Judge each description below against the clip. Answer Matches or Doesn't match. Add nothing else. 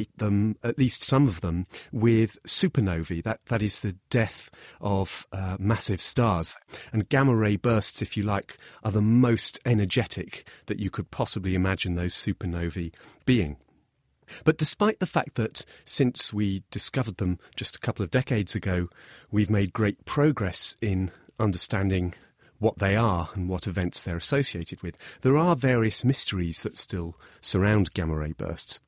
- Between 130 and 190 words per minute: Matches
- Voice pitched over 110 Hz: Doesn't match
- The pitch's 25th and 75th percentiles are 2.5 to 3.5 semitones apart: Doesn't match